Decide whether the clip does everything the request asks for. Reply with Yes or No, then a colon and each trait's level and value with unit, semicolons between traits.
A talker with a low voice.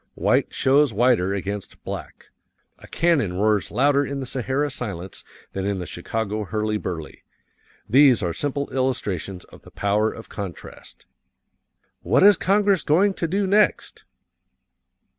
Yes: low, 115 Hz